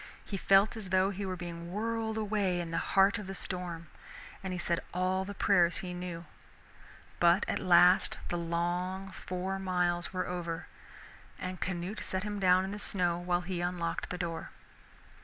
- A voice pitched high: No, medium, 180 Hz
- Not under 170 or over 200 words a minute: Yes, average, 175 wpm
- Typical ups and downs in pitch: No, narrow, 1.7 semitones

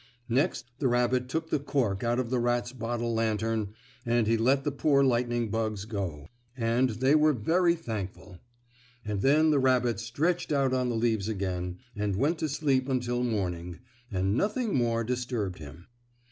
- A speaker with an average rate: Yes, average, 170 wpm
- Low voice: Yes, low, 120 Hz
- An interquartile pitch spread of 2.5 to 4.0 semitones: Yes, average, 3.7 semitones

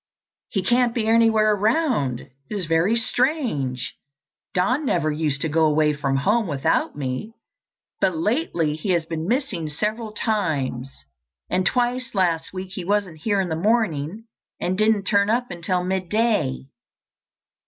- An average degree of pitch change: No, wide, 6.0 semitones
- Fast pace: No, average, 145 wpm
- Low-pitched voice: No, medium, 185 Hz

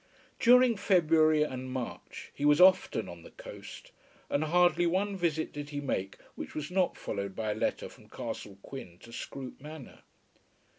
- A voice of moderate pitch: Yes, medium, 155 Hz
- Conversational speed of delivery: Yes, average, 165 wpm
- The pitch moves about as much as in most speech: No, wide, 5.7 semitones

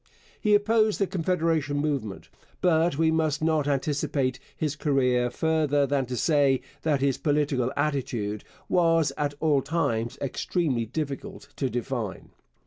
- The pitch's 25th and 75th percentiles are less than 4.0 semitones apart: Yes, average, 3.4 semitones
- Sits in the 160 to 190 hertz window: No, medium, 145 Hz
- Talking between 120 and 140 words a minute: Yes, slow, 135 wpm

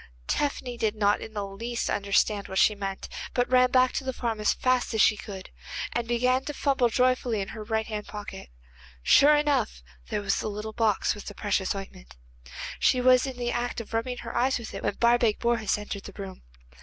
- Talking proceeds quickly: Yes, fast, 210 wpm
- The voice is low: No, high, 225 Hz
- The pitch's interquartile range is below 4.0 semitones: Yes, average, 3.4 semitones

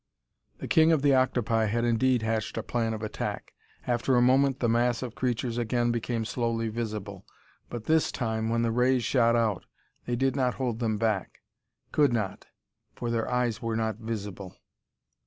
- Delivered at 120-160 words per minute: No, average, 175 wpm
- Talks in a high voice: No, low, 115 Hz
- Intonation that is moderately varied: No, narrow, 1.9 semitones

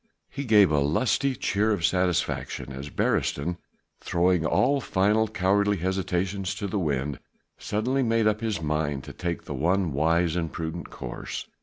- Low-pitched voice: Yes, very low, 90 Hz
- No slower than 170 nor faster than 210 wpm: No, average, 155 wpm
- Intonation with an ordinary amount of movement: Yes, average, 4.5 semitones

